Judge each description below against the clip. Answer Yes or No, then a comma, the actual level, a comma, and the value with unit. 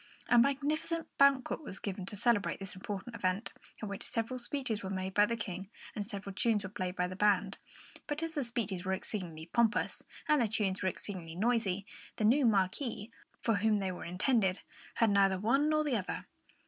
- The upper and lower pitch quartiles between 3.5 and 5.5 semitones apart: Yes, average, 4.1 semitones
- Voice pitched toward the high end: Yes, high, 210 Hz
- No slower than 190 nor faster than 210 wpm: Yes, average, 195 wpm